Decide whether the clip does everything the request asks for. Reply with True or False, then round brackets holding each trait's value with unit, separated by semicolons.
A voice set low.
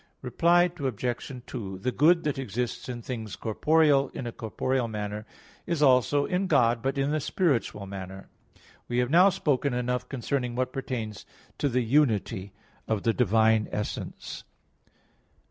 True (125 Hz)